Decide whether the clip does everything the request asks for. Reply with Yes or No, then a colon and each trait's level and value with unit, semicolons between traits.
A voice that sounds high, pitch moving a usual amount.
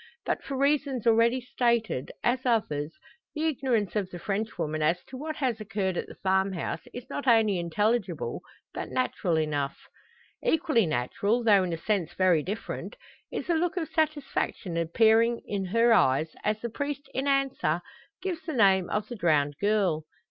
No: high, 215 Hz; wide, 6.5 semitones